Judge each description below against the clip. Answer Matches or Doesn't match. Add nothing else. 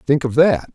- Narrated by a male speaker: Matches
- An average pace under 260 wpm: Matches